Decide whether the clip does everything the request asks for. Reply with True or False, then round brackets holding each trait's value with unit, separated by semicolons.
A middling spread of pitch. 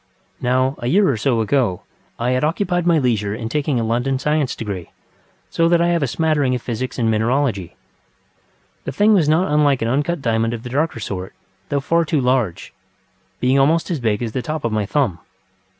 True (5.0 semitones)